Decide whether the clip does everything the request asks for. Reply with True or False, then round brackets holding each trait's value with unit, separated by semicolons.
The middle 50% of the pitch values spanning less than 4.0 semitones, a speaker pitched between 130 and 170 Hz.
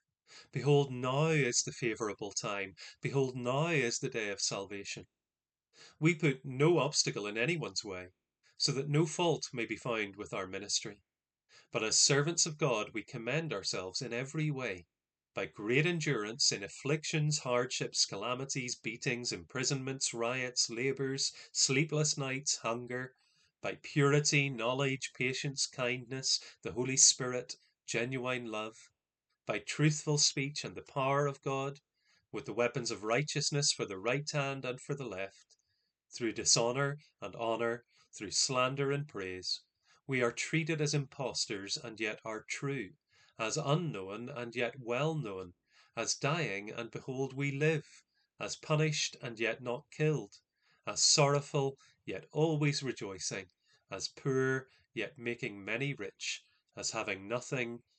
True (3.5 semitones; 135 Hz)